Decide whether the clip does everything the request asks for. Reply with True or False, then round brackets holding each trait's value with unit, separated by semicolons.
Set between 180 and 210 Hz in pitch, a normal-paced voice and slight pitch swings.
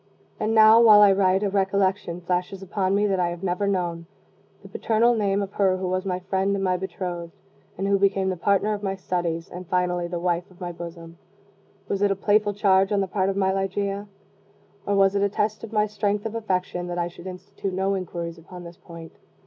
False (190 Hz; 220 wpm; 2.2 semitones)